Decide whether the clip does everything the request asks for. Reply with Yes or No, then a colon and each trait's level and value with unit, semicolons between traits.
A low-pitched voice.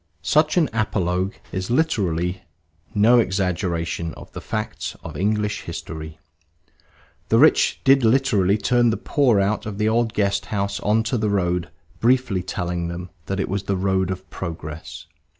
Yes: low, 100 Hz